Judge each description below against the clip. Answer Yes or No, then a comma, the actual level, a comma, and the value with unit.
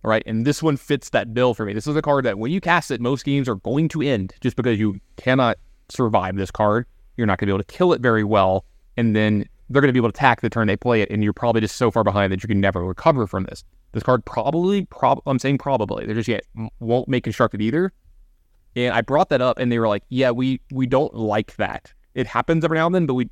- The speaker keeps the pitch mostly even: No, average, 4.3 semitones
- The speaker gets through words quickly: Yes, fast, 275 wpm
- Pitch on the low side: Yes, low, 115 Hz